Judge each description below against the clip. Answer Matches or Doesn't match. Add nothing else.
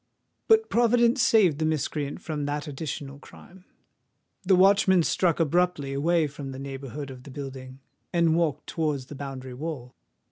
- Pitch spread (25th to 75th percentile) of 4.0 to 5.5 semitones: Matches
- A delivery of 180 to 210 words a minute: Doesn't match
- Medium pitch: Matches